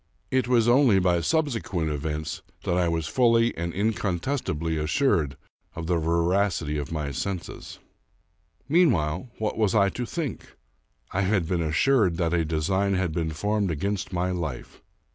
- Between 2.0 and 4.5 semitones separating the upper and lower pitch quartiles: No, average, 5.0 semitones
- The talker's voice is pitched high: No, very low, 90 Hz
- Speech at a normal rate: Yes, average, 155 wpm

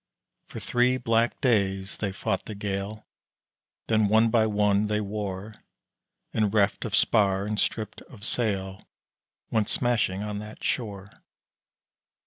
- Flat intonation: Yes, narrow, 1.8 semitones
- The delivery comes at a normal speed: No, slow, 130 wpm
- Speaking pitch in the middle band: No, low, 105 Hz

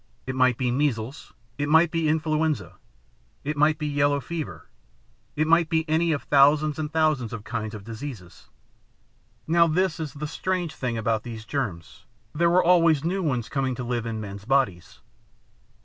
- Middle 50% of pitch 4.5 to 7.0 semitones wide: Yes, average, 5.1 semitones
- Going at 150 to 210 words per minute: Yes, average, 170 wpm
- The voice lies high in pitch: No, medium, 145 Hz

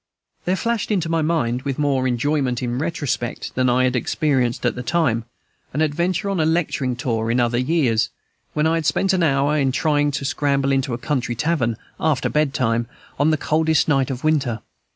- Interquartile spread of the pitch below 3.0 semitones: No, average, 4.0 semitones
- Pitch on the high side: No, medium, 140 Hz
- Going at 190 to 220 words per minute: Yes, average, 200 wpm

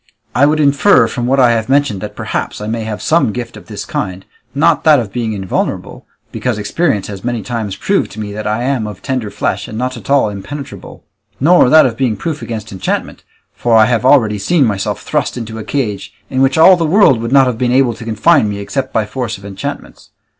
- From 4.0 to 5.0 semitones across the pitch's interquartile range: Yes, average, 4.3 semitones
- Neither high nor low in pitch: No, low, 120 Hz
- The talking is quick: Yes, fast, 225 wpm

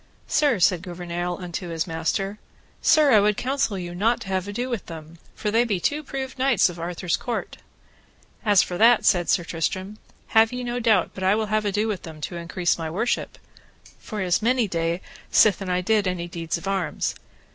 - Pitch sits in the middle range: No, high, 195 Hz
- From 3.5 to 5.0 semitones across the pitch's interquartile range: Yes, average, 4.3 semitones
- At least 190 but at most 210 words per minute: Yes, average, 200 wpm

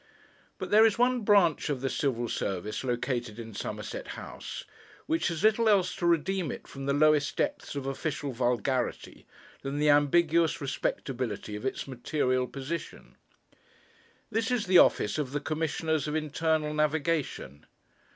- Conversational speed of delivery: Yes, average, 150 wpm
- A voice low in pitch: No, medium, 150 Hz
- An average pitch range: Yes, average, 4.5 semitones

